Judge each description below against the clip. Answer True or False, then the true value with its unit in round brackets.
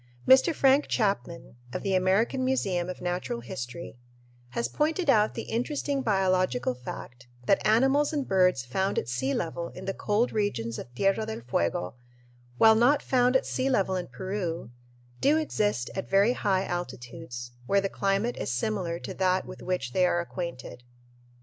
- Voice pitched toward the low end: False (190 Hz)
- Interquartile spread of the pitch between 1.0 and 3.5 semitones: False (5.4 semitones)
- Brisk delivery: False (165 wpm)